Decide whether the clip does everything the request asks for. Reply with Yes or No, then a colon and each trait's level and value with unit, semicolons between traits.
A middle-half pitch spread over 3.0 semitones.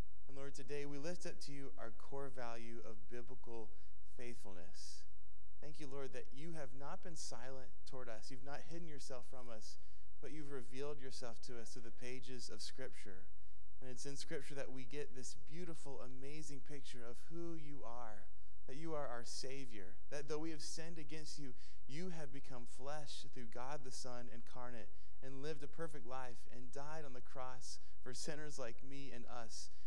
Yes: average, 4.0 semitones